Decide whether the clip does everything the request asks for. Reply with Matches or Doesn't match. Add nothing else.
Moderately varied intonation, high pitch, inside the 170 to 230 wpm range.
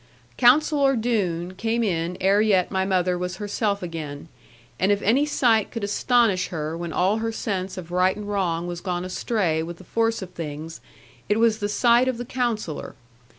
Matches